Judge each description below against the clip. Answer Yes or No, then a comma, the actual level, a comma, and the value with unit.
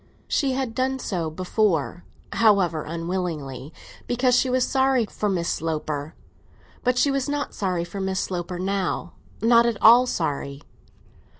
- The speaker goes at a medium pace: No, slow, 125 wpm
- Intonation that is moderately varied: No, wide, 6.9 semitones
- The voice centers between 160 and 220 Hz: Yes, high, 190 Hz